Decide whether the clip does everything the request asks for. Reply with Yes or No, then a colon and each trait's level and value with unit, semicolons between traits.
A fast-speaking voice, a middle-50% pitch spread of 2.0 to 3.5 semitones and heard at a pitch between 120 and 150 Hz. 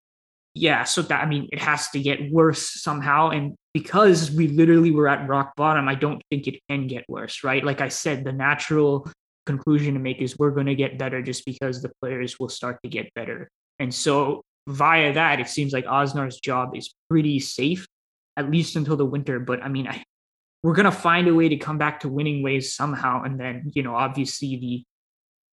Yes: fast, 210 wpm; narrow, 2.5 semitones; medium, 140 Hz